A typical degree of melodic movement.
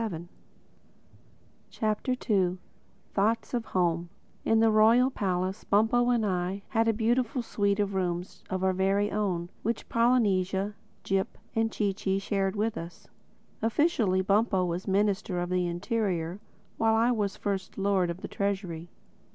Yes: average, 3.3 semitones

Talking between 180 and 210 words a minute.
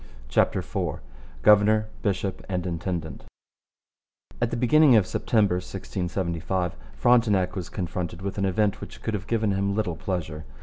No: average, 140 wpm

